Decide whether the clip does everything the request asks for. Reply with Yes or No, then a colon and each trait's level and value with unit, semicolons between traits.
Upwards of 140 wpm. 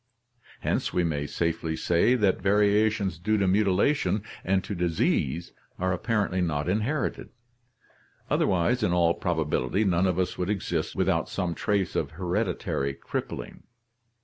No: slow, 135 wpm